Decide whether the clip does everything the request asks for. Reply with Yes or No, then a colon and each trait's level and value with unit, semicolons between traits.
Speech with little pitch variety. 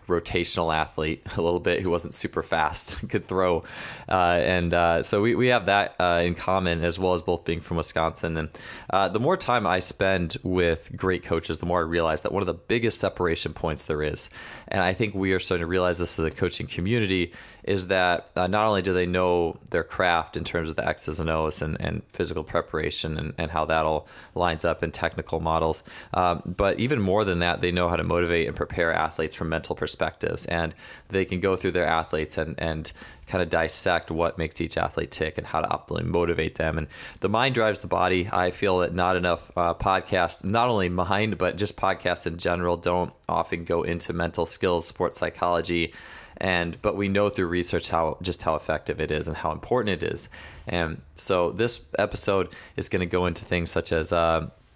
Yes: narrow, 2.1 semitones